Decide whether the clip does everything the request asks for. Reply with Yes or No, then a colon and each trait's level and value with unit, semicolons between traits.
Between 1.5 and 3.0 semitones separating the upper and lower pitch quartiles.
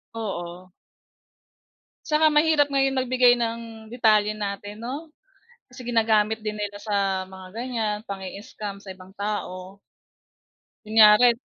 No: average, 3.5 semitones